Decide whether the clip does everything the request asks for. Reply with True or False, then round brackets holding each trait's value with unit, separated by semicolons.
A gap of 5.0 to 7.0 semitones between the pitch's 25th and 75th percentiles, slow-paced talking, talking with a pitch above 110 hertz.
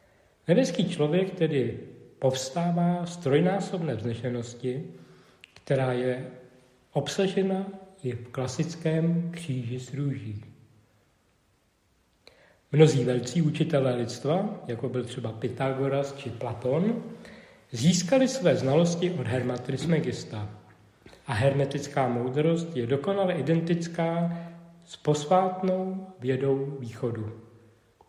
True (5.5 semitones; 90 wpm; 140 Hz)